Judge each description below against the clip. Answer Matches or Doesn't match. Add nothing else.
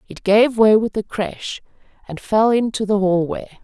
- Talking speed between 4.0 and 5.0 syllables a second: Matches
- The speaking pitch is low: Doesn't match